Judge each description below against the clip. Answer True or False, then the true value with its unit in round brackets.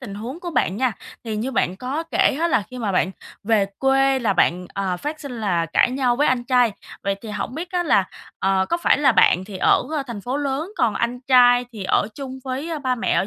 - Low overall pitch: False (245 Hz)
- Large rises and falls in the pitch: False (4.8 semitones)